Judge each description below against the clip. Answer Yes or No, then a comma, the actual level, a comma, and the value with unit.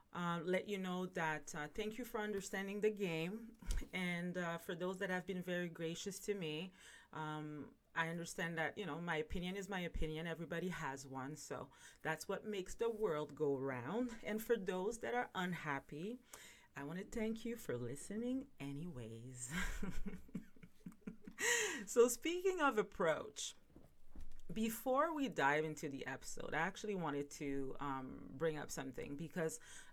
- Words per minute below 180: Yes, average, 155 wpm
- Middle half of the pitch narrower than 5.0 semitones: No, wide, 5.5 semitones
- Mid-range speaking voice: Yes, medium, 180 Hz